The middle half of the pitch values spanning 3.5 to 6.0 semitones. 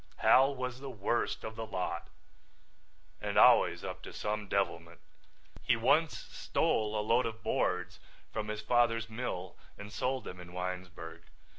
Yes: average, 4.7 semitones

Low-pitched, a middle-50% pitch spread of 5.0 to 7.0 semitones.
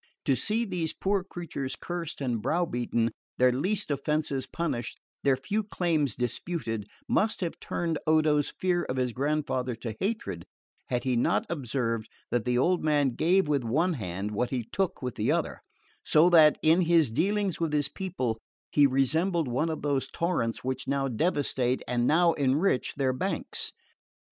No: medium, 145 Hz; average, 5.3 semitones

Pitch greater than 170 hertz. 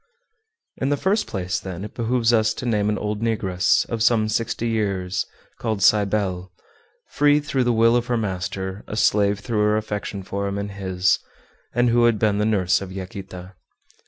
No: low, 105 Hz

